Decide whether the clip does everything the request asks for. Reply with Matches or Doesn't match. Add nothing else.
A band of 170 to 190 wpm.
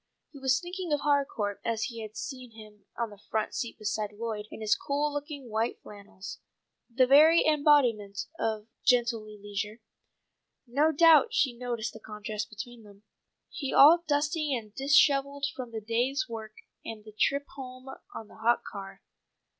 Doesn't match